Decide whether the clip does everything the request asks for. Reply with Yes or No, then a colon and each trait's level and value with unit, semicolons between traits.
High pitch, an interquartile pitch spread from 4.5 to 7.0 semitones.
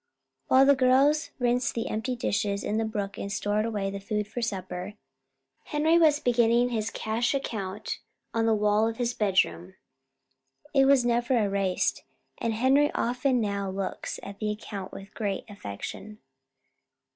No: high, 220 Hz; average, 3.6 semitones